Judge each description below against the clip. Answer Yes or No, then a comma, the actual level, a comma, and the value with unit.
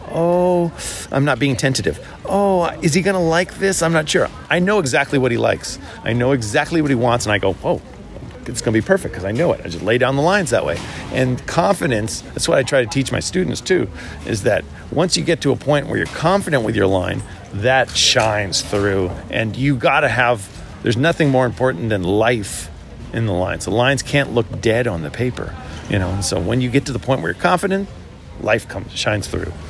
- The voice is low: Yes, low, 125 Hz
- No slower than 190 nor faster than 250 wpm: Yes, fast, 225 wpm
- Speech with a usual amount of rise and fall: No, wide, 7.3 semitones